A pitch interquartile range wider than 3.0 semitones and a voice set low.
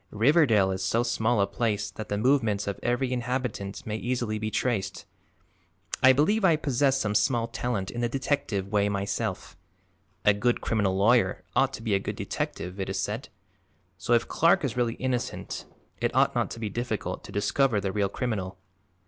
Yes: average, 3.7 semitones; low, 115 Hz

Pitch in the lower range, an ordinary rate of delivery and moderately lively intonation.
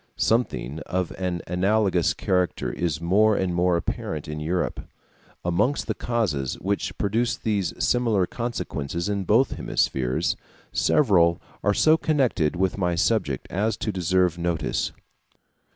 No: very low, 95 Hz; slow, 130 wpm; average, 4.1 semitones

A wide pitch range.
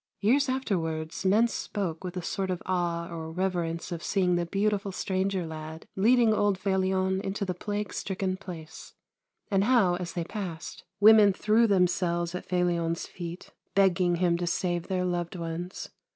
No: narrow, 2.4 semitones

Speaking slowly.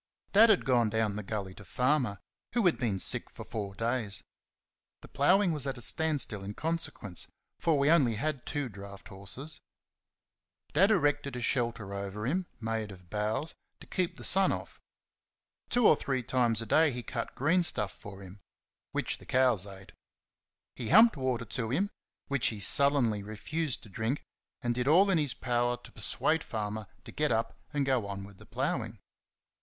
No: average, 180 wpm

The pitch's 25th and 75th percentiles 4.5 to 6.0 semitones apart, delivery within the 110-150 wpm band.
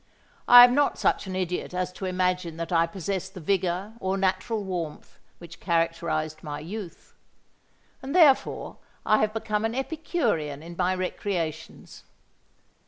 No: average, 4.1 semitones; average, 145 wpm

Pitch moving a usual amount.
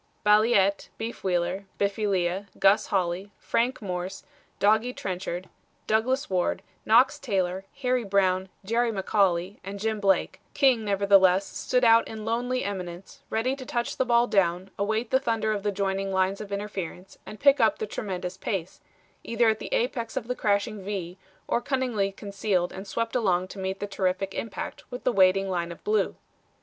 Yes: average, 3.3 semitones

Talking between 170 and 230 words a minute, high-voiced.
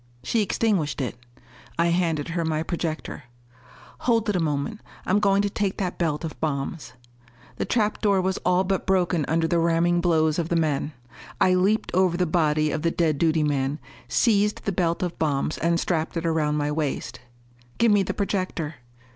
No: average, 185 wpm; medium, 170 Hz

